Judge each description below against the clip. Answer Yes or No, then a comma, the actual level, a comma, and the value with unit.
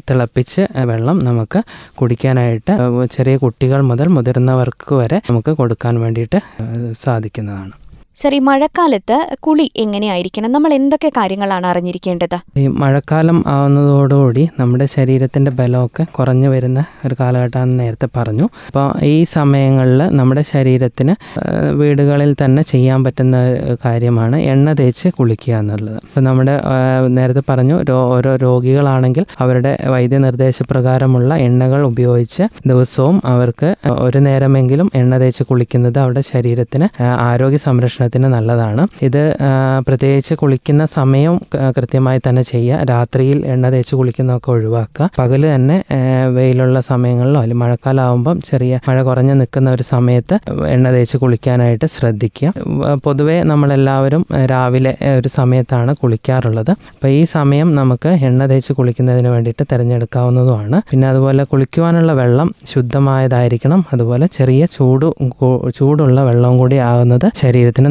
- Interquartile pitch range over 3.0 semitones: No, narrow, 2.5 semitones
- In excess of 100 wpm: Yes, average, 110 wpm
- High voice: No, low, 130 Hz